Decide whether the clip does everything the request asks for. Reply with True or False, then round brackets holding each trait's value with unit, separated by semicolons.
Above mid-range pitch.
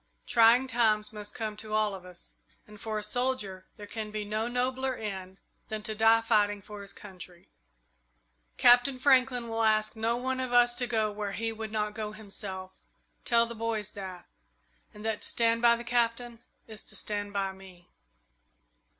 True (215 Hz)